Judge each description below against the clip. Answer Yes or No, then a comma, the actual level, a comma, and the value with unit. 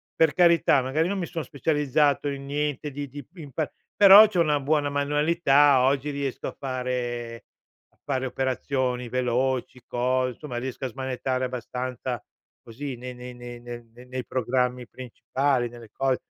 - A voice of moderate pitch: No, low, 130 Hz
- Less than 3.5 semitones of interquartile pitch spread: Yes, narrow, 2.6 semitones